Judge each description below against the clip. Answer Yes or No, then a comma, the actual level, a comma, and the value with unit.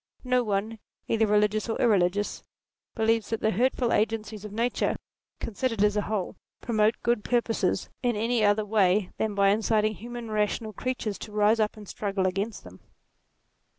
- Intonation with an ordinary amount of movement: No, narrow, 1.8 semitones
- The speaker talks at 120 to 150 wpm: No, average, 160 wpm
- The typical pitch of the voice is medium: No, high, 215 Hz